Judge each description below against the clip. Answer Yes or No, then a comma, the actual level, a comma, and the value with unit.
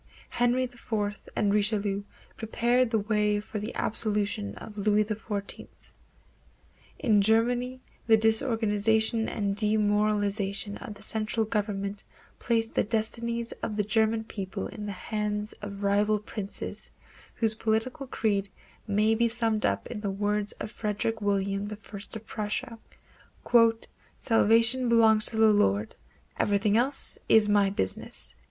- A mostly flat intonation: Yes, narrow, 1.7 semitones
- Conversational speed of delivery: No, slow, 130 wpm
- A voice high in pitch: Yes, high, 215 Hz